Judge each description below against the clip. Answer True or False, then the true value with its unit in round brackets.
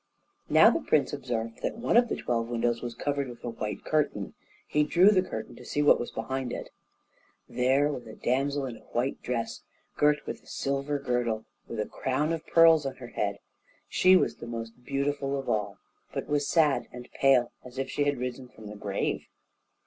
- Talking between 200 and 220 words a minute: True (205 wpm)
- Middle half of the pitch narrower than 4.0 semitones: True (3.5 semitones)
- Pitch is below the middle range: True (130 Hz)